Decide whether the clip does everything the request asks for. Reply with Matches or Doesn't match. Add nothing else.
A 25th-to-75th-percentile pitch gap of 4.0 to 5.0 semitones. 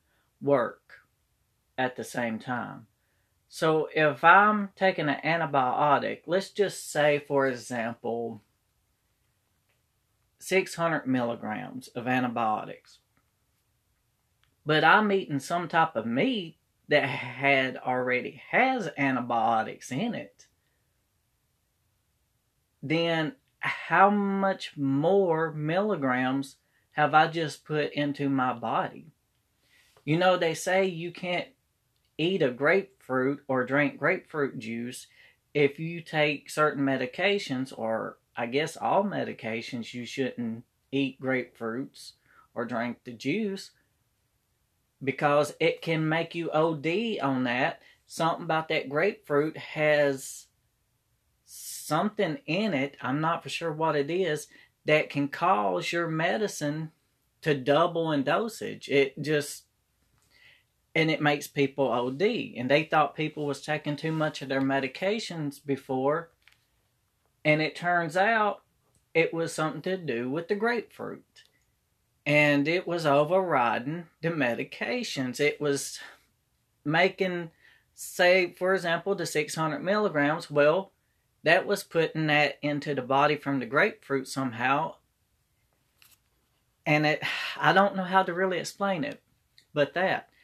Matches